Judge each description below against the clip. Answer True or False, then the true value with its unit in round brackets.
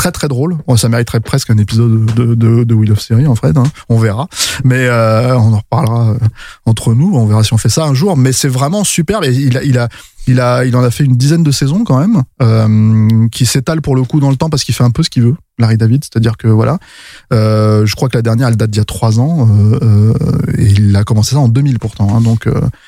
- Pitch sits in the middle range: False (120 Hz)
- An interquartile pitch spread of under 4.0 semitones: True (3.5 semitones)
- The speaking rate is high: True (270 wpm)